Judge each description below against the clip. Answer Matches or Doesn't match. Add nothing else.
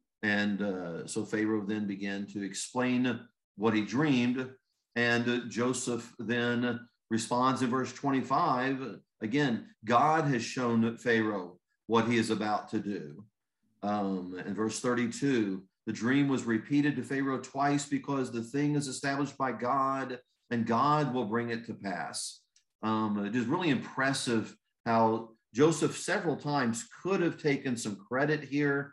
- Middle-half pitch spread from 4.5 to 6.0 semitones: Doesn't match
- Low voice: Matches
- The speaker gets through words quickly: Doesn't match